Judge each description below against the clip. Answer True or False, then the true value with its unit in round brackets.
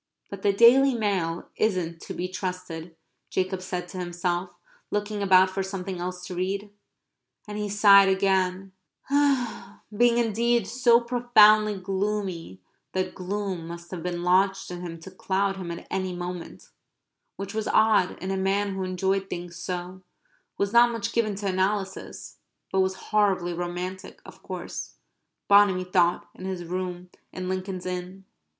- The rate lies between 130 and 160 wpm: True (150 wpm)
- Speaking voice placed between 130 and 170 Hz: False (190 Hz)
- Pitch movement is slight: True (2.1 semitones)